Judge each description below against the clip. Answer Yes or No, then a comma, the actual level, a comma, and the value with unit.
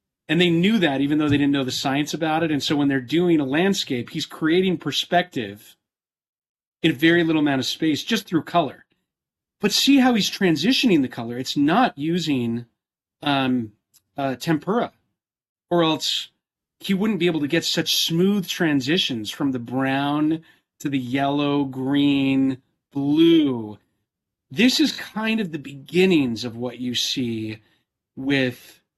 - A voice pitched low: No, medium, 150 Hz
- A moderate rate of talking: Yes, average, 155 wpm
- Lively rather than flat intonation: No, average, 4.3 semitones